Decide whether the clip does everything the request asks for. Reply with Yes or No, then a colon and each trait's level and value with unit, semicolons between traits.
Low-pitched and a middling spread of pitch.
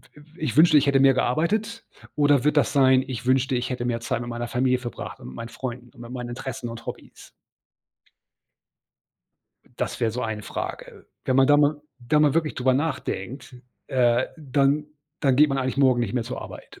Yes: low, 130 Hz; average, 3.0 semitones